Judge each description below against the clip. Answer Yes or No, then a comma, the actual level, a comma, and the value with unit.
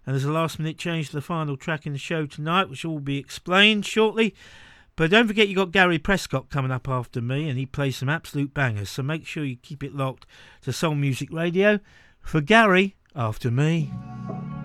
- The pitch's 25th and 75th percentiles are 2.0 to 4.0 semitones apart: No, average, 4.7 semitones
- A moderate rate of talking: No, fast, 210 wpm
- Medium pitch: Yes, medium, 150 Hz